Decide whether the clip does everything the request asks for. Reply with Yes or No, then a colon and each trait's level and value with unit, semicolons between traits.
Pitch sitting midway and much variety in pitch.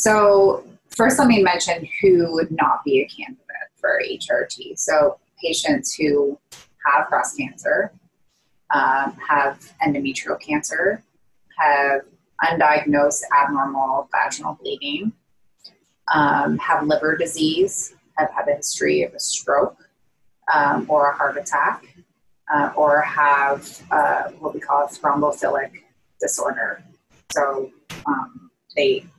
Yes: medium, 165 Hz; wide, 8.6 semitones